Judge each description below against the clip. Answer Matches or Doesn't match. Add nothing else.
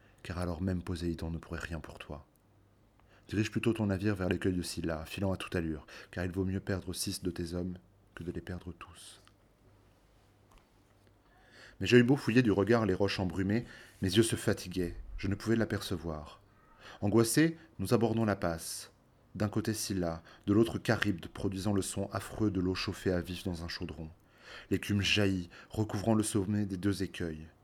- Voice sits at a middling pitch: Doesn't match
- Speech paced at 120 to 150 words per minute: Doesn't match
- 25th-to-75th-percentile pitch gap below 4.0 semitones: Matches